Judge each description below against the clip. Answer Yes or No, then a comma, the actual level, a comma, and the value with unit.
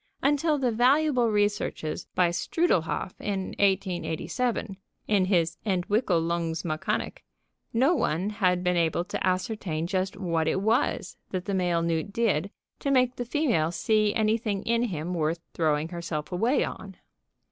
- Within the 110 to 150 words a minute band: Yes, slow, 135 wpm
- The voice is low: No, high, 190 Hz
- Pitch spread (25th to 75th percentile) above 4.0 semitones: Yes, average, 5.1 semitones